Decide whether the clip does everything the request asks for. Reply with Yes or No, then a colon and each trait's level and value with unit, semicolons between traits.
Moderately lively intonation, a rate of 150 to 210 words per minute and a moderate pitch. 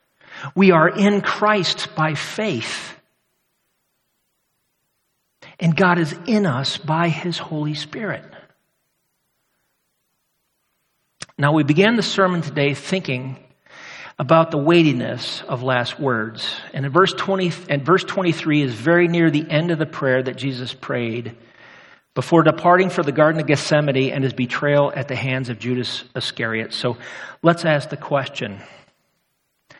No: average, 4.6 semitones; slow, 135 wpm; medium, 150 Hz